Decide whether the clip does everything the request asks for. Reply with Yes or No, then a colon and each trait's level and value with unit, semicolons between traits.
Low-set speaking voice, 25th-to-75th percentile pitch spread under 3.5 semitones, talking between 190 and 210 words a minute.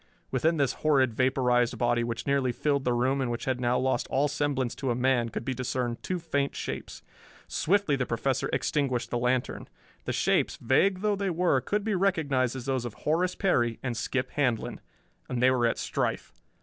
Yes: low, 130 Hz; average, 3.1 semitones; average, 195 wpm